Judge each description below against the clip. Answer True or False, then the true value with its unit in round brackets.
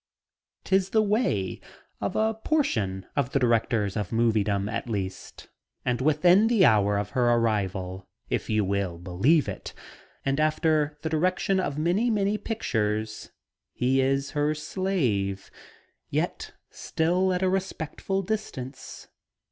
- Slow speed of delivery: True (130 wpm)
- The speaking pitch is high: False (135 Hz)